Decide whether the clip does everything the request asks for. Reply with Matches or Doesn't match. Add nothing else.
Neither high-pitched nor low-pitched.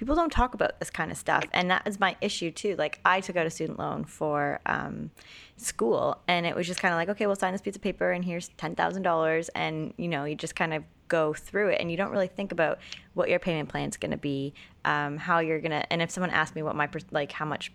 Matches